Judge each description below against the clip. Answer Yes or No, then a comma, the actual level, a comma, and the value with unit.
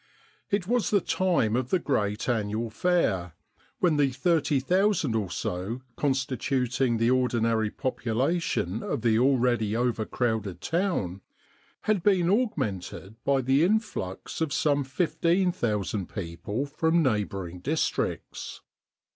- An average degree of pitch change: No, wide, 7.2 semitones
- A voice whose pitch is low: Yes, low, 130 Hz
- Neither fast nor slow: No, slow, 115 wpm